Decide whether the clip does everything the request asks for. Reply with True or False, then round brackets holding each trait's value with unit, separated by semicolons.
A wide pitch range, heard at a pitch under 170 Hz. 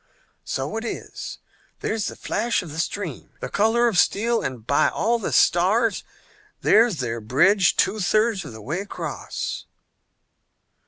False (6.9 semitones; 200 Hz)